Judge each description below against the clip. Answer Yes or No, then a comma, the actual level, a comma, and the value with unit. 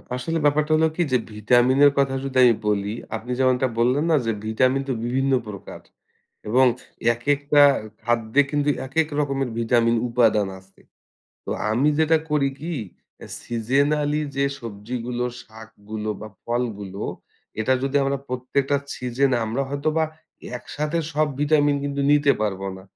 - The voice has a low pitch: Yes, low, 130 Hz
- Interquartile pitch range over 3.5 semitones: Yes, average, 3.9 semitones